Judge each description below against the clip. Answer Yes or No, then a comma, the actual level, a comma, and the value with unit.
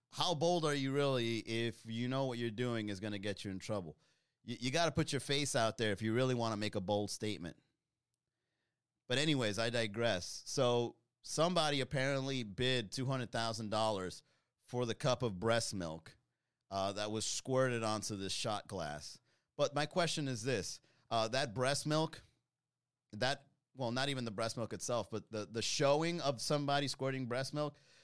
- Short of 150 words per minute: No, average, 180 wpm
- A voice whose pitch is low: Yes, low, 120 Hz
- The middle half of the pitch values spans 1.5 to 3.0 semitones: No, average, 4.2 semitones